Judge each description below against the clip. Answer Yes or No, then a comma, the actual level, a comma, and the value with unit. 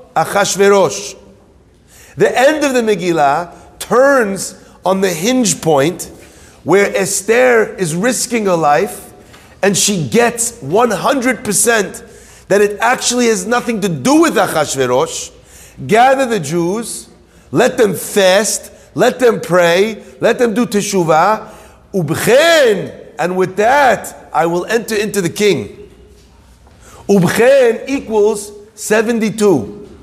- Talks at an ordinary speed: No, slow, 110 wpm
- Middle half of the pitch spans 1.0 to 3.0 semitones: No, average, 4.3 semitones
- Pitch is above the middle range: Yes, high, 210 Hz